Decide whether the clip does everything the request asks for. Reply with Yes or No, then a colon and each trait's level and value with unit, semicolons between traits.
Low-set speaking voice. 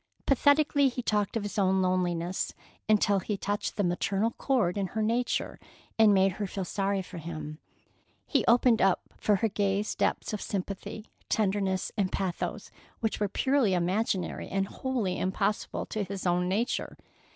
No: high, 200 Hz